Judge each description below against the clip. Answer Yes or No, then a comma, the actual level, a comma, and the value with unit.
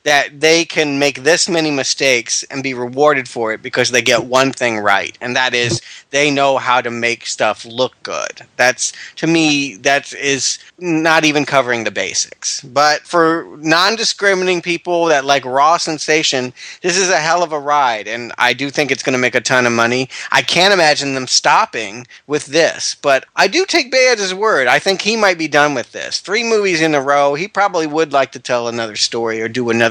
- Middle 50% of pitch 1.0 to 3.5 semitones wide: No, average, 4.6 semitones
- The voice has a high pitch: No, medium, 140 Hz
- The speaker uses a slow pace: No, fast, 205 wpm